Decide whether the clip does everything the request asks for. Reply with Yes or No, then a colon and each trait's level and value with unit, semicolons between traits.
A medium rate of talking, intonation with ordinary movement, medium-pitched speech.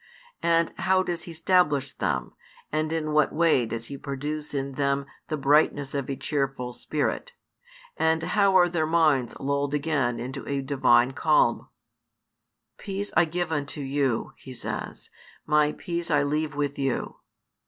Yes: average, 155 wpm; average, 3.0 semitones; medium, 145 Hz